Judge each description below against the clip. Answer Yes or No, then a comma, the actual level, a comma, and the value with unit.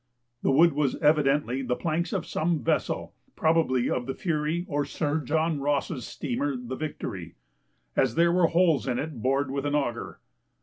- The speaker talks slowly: No, average, 170 wpm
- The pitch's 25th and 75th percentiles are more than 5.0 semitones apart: No, average, 3.2 semitones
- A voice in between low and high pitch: Yes, medium, 145 Hz